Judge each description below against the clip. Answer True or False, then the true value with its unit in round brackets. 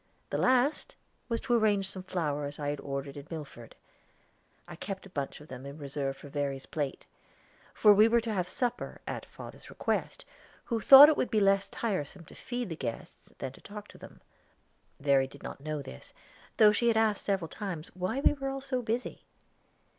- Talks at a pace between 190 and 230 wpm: True (200 wpm)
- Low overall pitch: False (185 Hz)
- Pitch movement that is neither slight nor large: False (7.7 semitones)